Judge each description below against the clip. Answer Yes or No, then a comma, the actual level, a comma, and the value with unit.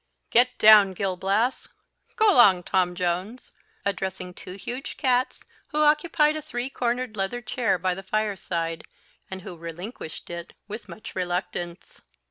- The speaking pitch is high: Yes, high, 200 Hz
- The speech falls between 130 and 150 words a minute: Yes, average, 140 wpm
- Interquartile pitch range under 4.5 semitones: No, wide, 5.4 semitones